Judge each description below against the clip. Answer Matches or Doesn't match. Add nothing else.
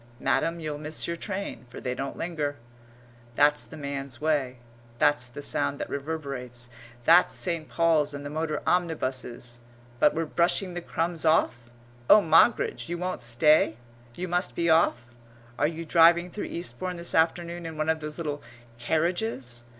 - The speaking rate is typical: Matches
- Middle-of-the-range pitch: Matches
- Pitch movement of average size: Matches